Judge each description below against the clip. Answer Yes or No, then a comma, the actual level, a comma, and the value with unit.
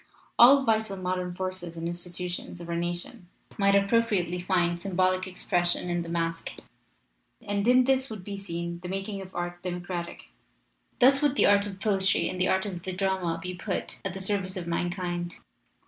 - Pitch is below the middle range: No, medium, 185 Hz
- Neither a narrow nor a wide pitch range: No, narrow, 2.2 semitones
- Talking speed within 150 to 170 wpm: No, average, 180 wpm